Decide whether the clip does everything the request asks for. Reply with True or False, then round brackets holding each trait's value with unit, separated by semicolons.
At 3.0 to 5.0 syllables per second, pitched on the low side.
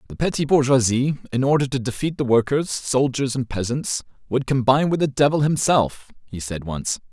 False (5.3 syllables/s; 130 Hz)